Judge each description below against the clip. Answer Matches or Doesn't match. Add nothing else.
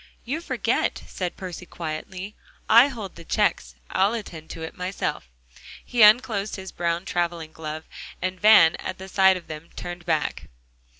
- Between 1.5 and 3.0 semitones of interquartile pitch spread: Doesn't match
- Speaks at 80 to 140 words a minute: Doesn't match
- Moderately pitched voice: Matches